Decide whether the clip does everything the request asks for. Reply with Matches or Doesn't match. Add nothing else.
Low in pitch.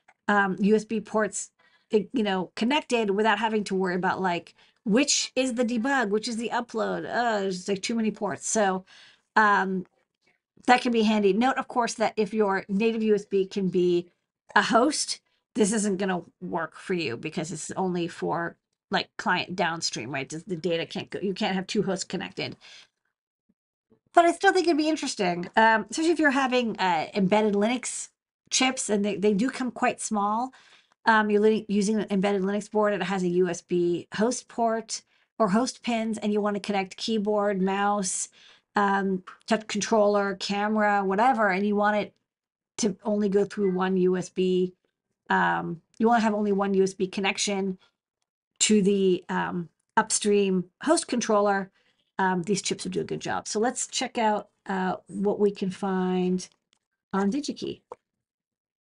Doesn't match